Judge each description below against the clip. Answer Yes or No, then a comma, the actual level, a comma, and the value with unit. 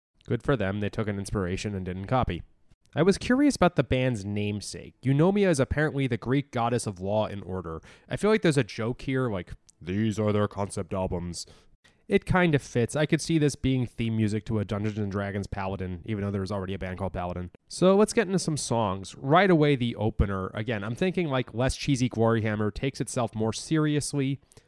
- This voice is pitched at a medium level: No, low, 115 Hz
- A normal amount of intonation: No, wide, 5.9 semitones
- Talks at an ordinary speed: No, fast, 210 wpm